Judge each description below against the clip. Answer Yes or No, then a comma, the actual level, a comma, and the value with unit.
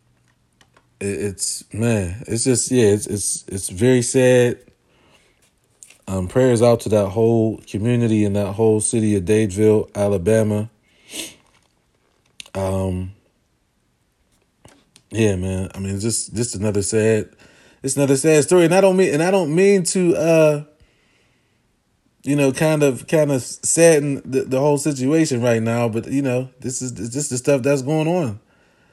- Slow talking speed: No, average, 150 wpm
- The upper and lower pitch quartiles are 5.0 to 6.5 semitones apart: Yes, average, 5.3 semitones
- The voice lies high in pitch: No, low, 120 Hz